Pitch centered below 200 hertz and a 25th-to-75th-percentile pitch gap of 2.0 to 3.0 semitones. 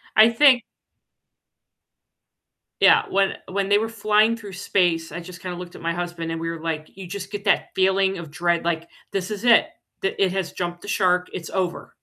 Yes: medium, 185 Hz; average, 2.7 semitones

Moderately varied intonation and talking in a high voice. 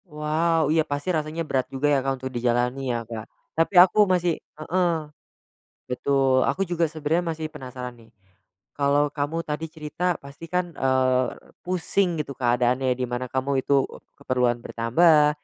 No: average, 4.1 semitones; medium, 145 Hz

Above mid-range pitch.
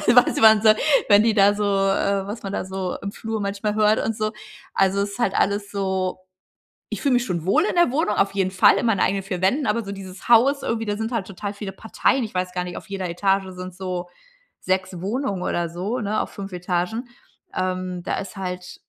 Yes: high, 200 Hz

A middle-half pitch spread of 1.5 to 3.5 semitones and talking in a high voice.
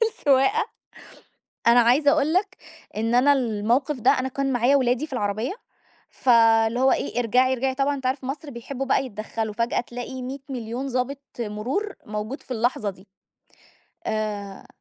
Yes: average, 3.2 semitones; very high, 250 Hz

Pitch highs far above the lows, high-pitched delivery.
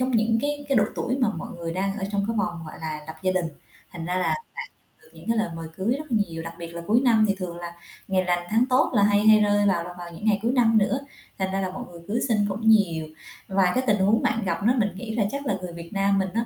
No: average, 4.2 semitones; high, 200 Hz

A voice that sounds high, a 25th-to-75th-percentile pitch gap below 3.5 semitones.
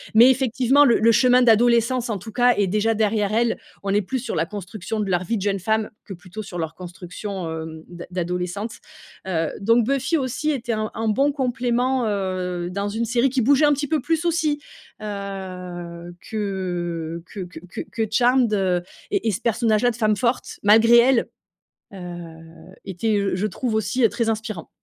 No: high, 215 Hz; average, 4.7 semitones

